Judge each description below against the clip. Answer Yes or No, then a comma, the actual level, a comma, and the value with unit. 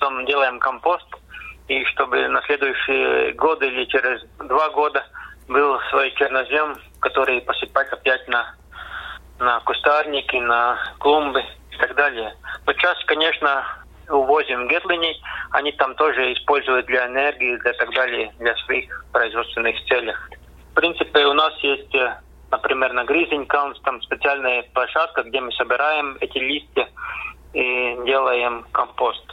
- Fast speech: No, average, 125 wpm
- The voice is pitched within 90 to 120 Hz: No, low, 135 Hz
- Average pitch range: Yes, average, 3.1 semitones